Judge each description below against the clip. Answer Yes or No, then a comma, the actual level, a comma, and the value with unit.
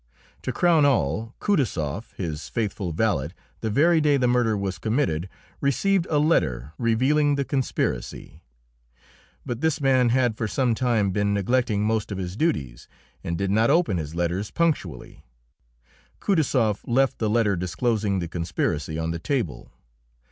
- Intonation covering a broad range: Yes, wide, 6.9 semitones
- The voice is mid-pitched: No, low, 110 Hz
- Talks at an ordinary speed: Yes, average, 150 wpm